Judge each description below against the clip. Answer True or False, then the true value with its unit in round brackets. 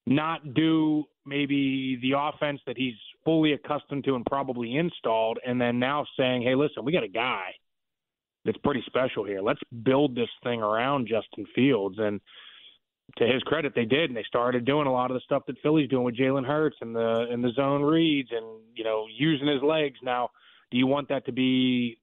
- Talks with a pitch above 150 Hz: False (135 Hz)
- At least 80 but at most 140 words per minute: False (200 wpm)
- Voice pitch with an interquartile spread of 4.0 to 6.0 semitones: False (3.1 semitones)